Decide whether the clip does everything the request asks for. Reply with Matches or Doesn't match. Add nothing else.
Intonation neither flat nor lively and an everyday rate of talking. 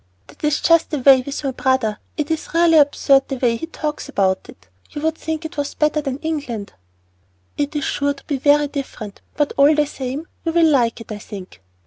Doesn't match